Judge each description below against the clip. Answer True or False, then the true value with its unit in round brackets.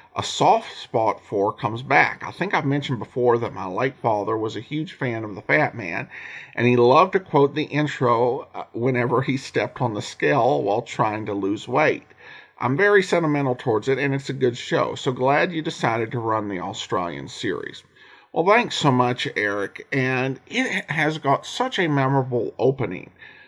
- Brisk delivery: False (185 wpm)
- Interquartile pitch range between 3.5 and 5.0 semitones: True (4.0 semitones)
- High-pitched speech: False (135 Hz)